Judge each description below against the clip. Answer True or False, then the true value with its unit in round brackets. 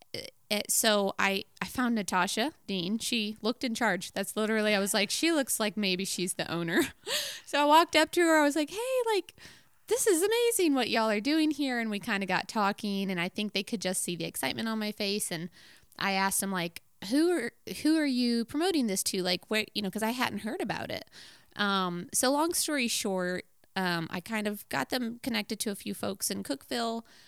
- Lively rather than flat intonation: True (6.0 semitones)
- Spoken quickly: True (220 wpm)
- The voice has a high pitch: True (215 Hz)